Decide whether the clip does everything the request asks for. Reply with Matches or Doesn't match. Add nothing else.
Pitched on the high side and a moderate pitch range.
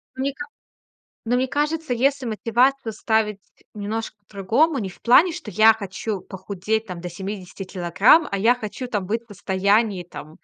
Matches